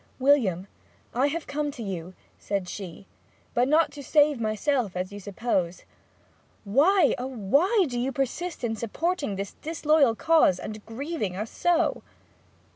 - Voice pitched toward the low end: No, very high, 250 Hz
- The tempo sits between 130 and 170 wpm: Yes, average, 145 wpm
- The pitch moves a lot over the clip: Yes, wide, 6.8 semitones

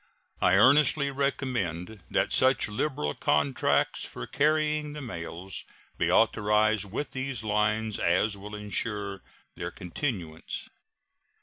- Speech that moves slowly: Yes, slow, 110 wpm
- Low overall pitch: Yes, low, 105 Hz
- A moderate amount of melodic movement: No, wide, 5.7 semitones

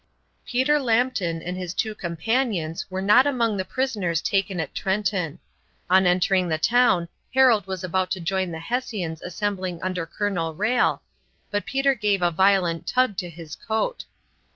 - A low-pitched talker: No, high, 190 Hz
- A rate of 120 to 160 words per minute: Yes, average, 155 wpm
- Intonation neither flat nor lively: Yes, average, 4.4 semitones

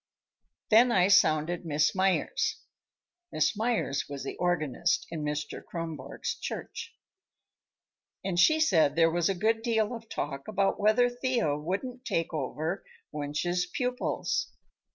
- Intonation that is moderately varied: No, wide, 6.2 semitones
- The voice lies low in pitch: No, medium, 180 Hz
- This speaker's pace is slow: Yes, slow, 130 wpm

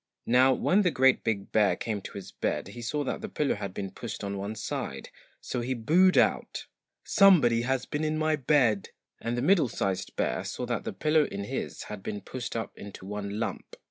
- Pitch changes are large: Yes, wide, 6.3 semitones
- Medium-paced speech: No, fast, 210 wpm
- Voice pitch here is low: Yes, low, 120 Hz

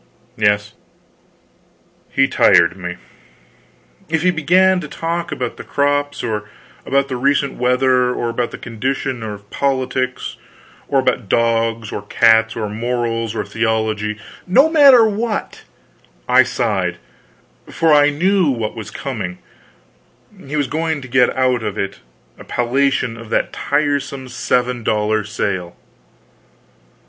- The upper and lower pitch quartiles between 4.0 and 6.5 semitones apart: Yes, average, 4.4 semitones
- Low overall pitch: Yes, low, 125 Hz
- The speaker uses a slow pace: Yes, slow, 130 wpm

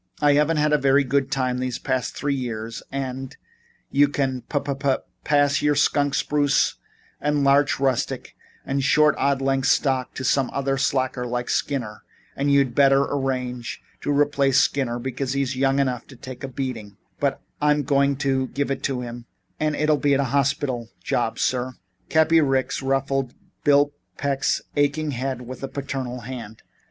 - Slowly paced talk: No, average, 170 wpm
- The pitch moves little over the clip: Yes, narrow, 1.8 semitones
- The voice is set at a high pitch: No, low, 135 Hz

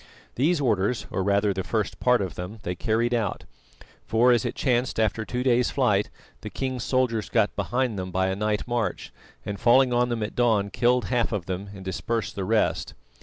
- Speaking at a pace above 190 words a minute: Yes, average, 200 wpm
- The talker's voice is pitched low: Yes, low, 115 Hz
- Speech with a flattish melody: No, average, 3.5 semitones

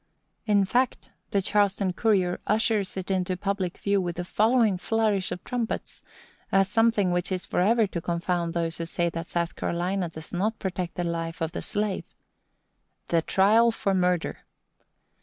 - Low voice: No, high, 190 Hz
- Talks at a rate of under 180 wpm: Yes, average, 160 wpm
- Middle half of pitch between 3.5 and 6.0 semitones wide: No, average, 3.1 semitones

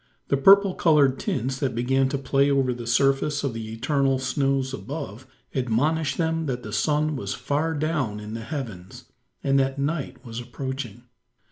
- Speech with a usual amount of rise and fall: Yes, average, 3.1 semitones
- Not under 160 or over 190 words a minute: Yes, average, 165 wpm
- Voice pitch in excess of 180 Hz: No, low, 135 Hz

